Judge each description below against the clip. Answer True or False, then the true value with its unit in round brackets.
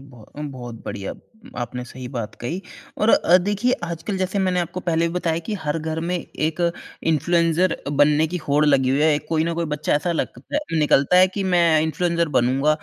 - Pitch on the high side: False (160 Hz)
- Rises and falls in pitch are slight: False (3.4 semitones)